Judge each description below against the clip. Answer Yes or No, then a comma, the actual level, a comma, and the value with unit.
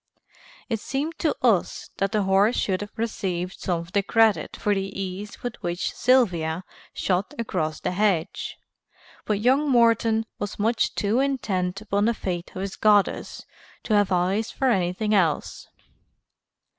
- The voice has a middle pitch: No, high, 205 Hz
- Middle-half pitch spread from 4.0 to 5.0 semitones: No, average, 3.5 semitones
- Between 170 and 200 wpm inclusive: No, average, 155 wpm